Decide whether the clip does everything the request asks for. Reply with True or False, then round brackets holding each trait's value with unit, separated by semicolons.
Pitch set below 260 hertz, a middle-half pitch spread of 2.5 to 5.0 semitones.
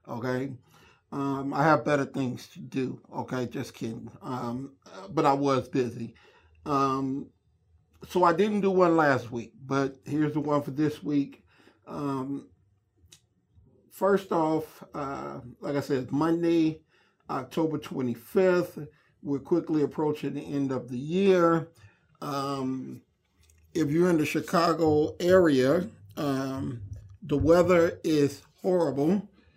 True (140 Hz; 3.9 semitones)